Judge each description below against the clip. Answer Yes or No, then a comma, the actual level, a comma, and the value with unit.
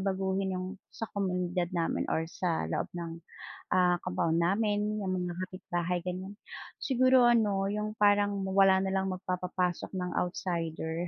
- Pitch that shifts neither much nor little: No, narrow, 2.1 semitones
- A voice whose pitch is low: No, medium, 185 Hz